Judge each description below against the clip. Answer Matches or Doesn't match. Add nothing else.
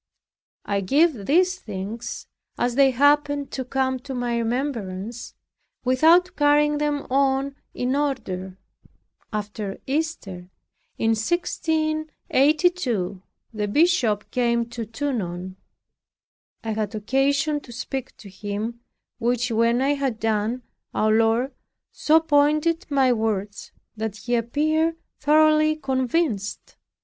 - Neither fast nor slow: Doesn't match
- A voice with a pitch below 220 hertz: Doesn't match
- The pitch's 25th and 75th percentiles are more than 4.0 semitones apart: Matches